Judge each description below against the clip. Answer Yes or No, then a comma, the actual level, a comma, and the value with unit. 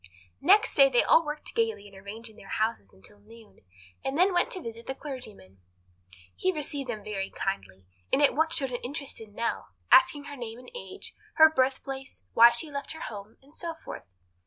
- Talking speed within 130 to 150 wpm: No, average, 195 wpm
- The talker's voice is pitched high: Yes, very high, 255 Hz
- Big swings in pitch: Yes, wide, 5.8 semitones